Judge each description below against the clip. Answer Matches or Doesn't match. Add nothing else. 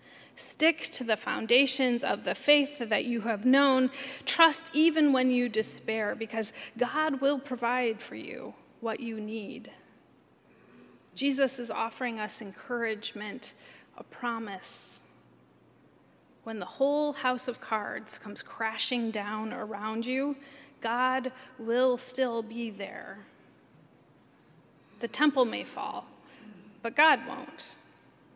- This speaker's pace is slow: Matches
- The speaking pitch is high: Matches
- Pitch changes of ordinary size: Matches